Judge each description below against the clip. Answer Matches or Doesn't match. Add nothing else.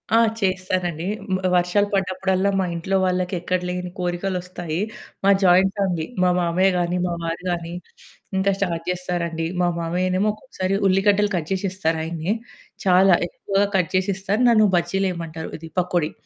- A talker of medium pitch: Matches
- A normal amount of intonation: Doesn't match